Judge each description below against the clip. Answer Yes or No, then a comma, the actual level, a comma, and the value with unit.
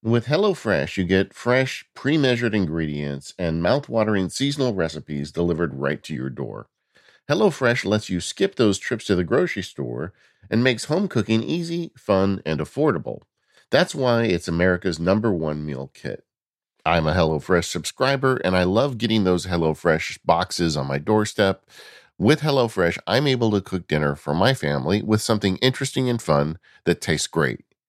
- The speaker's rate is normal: Yes, average, 160 wpm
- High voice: No, low, 100 Hz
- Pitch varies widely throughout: Yes, wide, 7.1 semitones